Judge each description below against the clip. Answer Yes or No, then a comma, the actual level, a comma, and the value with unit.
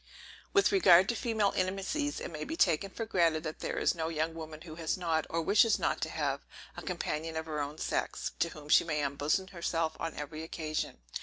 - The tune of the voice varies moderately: Yes, average, 3.4 semitones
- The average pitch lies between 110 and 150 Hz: No, medium, 165 Hz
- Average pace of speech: No, fast, 215 wpm